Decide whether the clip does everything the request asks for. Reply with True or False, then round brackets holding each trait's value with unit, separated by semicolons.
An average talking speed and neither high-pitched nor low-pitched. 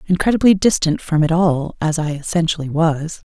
True (165 wpm; 165 Hz)